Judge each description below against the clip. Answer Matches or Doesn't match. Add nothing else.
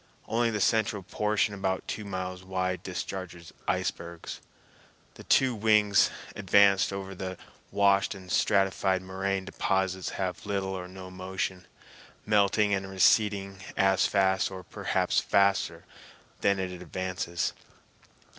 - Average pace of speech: Doesn't match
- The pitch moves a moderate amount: Doesn't match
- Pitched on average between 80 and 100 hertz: Matches